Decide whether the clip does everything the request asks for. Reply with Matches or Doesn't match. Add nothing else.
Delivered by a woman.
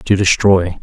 Doesn't match